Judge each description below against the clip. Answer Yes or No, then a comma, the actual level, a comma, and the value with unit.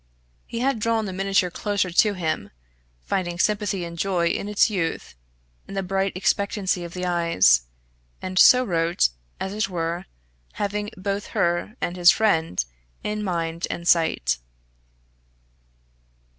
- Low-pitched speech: No, medium, 185 Hz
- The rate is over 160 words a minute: No, average, 140 wpm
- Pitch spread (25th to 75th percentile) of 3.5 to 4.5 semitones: No, average, 3.1 semitones